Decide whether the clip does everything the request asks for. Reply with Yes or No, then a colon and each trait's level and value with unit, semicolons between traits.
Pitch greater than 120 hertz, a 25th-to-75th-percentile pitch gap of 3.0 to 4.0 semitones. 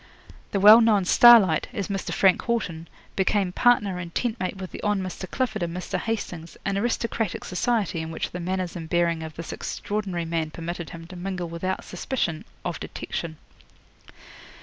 Yes: medium, 185 Hz; average, 3.5 semitones